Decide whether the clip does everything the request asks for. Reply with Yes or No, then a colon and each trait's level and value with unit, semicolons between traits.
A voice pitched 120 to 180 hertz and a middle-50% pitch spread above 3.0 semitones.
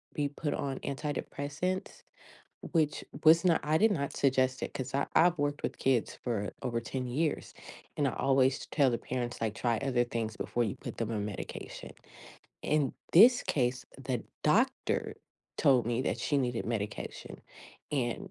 Yes: low, 135 Hz; average, 3.6 semitones